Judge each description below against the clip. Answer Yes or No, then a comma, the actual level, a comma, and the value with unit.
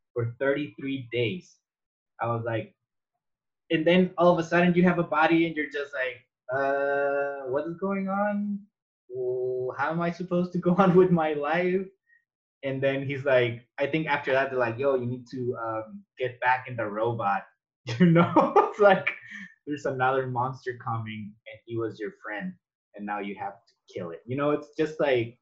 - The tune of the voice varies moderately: No, wide, 5.7 semitones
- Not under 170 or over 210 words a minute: Yes, average, 190 wpm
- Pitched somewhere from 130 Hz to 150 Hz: Yes, medium, 140 Hz